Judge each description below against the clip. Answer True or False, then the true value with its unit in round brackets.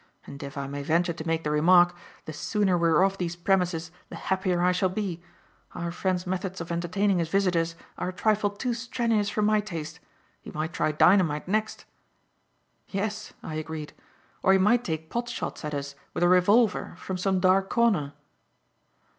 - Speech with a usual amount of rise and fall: True (3.6 semitones)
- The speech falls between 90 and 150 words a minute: False (185 wpm)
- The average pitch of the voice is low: False (180 Hz)